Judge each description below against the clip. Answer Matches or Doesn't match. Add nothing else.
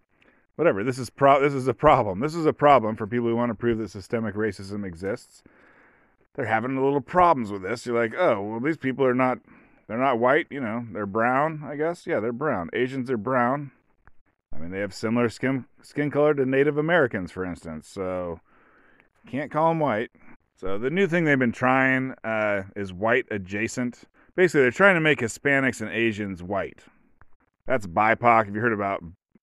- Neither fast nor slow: Matches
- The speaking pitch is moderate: Doesn't match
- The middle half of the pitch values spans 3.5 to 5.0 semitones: Matches